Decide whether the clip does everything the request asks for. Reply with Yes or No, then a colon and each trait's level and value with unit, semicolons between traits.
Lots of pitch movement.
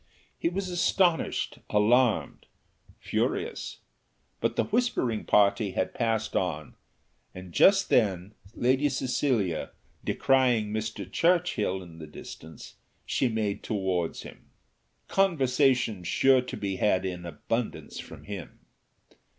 Yes: wide, 5.9 semitones